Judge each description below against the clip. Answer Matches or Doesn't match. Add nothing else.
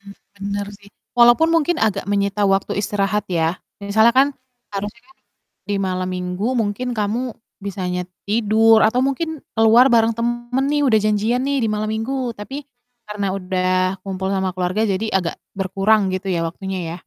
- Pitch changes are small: Doesn't match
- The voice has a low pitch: Doesn't match